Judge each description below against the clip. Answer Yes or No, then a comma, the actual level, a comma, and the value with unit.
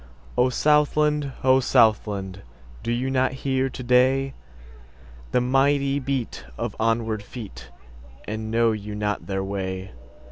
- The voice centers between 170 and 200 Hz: No, low, 115 Hz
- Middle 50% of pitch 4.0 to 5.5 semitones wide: Yes, average, 4.8 semitones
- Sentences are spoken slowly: Yes, slow, 110 wpm